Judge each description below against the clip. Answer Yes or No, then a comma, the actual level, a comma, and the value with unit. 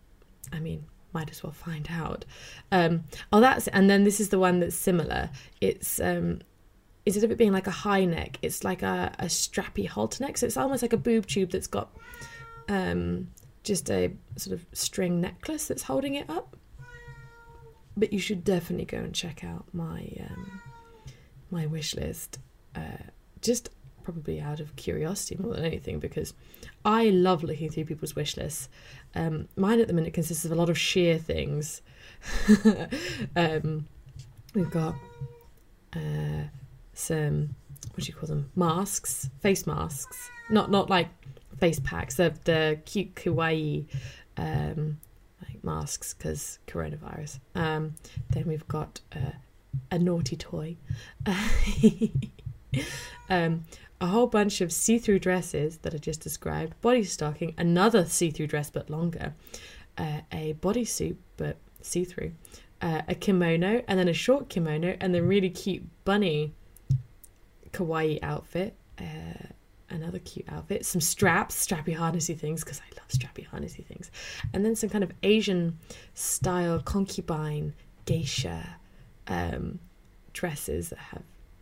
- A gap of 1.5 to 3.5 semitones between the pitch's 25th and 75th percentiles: No, average, 5.1 semitones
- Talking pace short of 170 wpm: Yes, average, 150 wpm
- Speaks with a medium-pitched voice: Yes, medium, 165 Hz